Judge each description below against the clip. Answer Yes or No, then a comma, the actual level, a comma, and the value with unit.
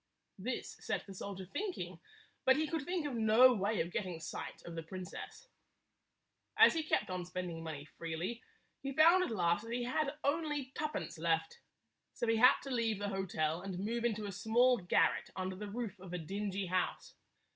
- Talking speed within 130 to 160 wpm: No, average, 190 wpm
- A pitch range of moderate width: No, wide, 5.9 semitones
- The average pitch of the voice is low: No, high, 205 Hz